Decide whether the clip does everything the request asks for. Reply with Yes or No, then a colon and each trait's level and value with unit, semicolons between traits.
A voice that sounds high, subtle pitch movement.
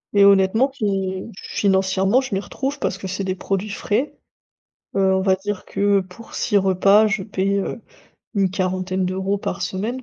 Yes: high, 195 Hz; narrow, 1.4 semitones